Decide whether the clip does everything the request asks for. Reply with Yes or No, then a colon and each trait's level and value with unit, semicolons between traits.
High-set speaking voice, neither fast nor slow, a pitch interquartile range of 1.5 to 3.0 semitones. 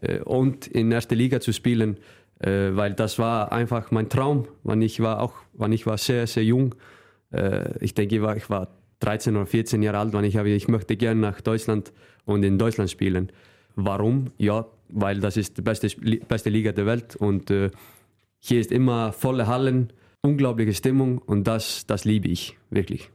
No: low, 110 Hz; average, 175 wpm; narrow, 2.4 semitones